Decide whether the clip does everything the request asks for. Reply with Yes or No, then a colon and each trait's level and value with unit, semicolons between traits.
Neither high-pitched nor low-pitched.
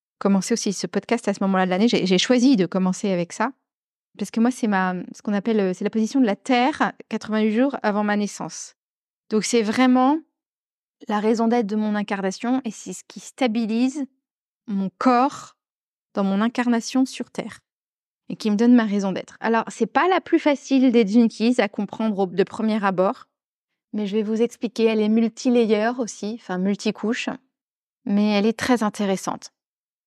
No: high, 220 Hz